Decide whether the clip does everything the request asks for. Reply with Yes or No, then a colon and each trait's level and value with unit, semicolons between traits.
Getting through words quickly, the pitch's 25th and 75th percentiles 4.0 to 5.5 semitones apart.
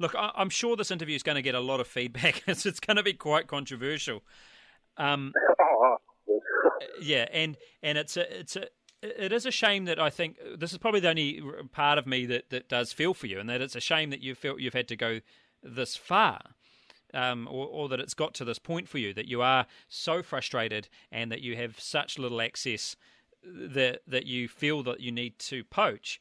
Yes: fast, 215 wpm; average, 5.2 semitones